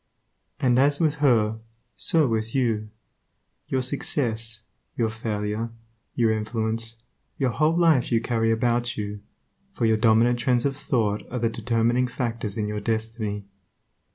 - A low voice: Yes, low, 115 Hz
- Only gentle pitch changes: Yes, narrow, 2.3 semitones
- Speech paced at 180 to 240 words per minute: No, average, 145 wpm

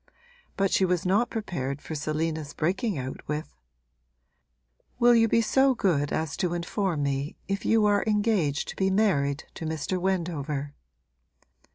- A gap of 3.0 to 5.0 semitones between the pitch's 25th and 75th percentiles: No, wide, 5.6 semitones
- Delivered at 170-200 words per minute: No, average, 150 wpm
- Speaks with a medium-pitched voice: Yes, medium, 175 Hz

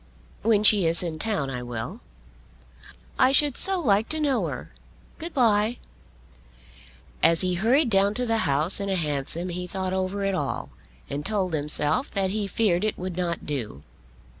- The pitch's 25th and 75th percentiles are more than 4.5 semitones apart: Yes, average, 5.1 semitones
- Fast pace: No, average, 170 wpm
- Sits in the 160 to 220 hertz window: Yes, high, 190 Hz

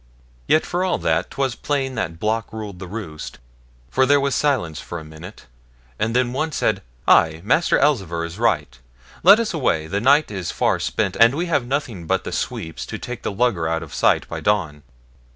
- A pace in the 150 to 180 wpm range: No, average, 200 wpm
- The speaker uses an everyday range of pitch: No, wide, 8.5 semitones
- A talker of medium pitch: No, low, 110 Hz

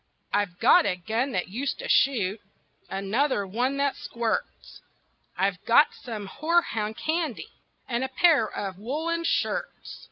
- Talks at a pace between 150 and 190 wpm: No, slow, 135 wpm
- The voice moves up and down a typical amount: No, wide, 5.8 semitones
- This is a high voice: Yes, high, 235 Hz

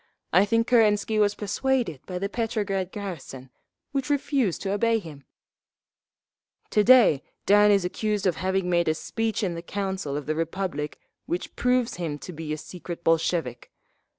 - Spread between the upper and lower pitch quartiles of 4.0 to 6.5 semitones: Yes, average, 4.6 semitones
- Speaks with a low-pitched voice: No, high, 190 Hz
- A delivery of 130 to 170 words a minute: Yes, average, 160 wpm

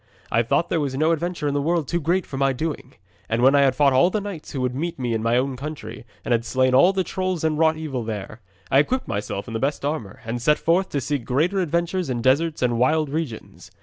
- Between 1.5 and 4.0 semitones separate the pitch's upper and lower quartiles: No, average, 4.6 semitones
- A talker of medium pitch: Yes, medium, 145 Hz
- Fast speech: Yes, fast, 255 wpm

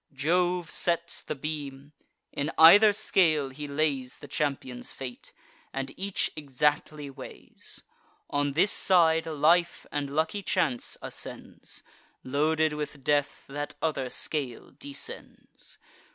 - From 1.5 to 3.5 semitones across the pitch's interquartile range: Yes, average, 2.7 semitones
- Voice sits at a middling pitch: Yes, medium, 150 Hz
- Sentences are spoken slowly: Yes, slow, 115 wpm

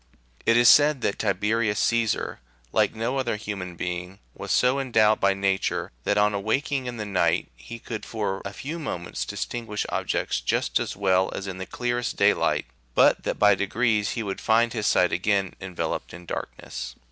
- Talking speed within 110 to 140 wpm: No, average, 180 wpm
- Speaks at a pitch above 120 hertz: No, low, 105 Hz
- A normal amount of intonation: Yes, average, 3.4 semitones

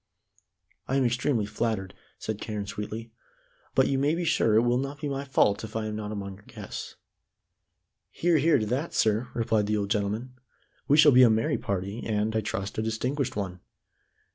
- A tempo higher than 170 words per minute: Yes, average, 190 wpm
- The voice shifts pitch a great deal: No, average, 4.1 semitones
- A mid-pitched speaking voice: No, low, 110 Hz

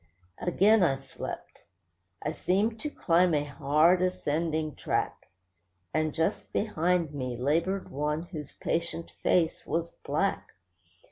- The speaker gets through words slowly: Yes, slow, 120 wpm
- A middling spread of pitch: Yes, average, 3.3 semitones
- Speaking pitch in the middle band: Yes, medium, 165 Hz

